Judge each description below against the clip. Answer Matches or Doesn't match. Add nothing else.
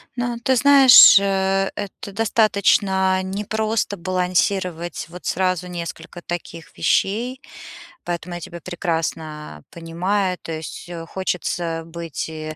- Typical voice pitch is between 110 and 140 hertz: Doesn't match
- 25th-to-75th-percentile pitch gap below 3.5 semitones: Matches